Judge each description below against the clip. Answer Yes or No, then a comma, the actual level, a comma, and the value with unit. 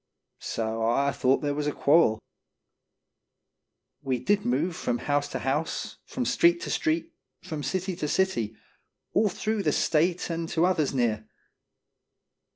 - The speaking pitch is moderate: Yes, medium, 150 Hz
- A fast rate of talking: No, average, 145 wpm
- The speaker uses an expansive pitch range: Yes, wide, 5.9 semitones